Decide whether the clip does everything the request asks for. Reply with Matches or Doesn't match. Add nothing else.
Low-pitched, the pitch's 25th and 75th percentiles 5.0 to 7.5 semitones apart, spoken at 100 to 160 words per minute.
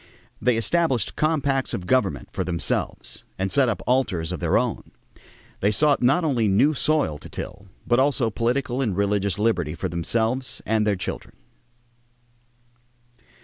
Matches